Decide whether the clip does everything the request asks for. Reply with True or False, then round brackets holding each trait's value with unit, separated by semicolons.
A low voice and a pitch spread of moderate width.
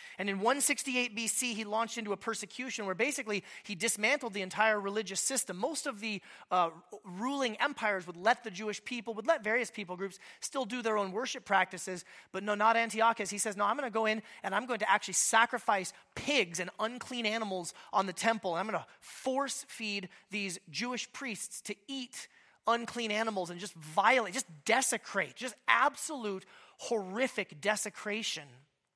False (215 Hz; 3.4 semitones)